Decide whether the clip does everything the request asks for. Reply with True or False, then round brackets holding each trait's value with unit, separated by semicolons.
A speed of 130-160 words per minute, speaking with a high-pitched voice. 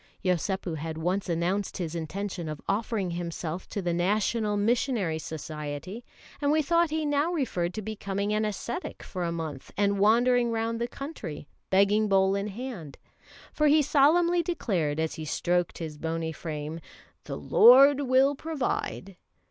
True (155 wpm; 200 Hz)